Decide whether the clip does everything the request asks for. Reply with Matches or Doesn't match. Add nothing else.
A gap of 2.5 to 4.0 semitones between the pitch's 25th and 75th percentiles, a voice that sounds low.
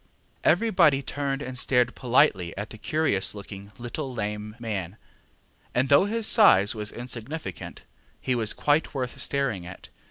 Doesn't match